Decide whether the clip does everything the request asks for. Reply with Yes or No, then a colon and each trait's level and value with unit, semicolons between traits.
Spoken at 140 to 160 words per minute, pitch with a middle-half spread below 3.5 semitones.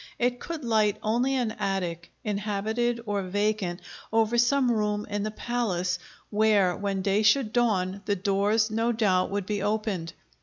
Yes: average, 155 wpm; narrow, 2.5 semitones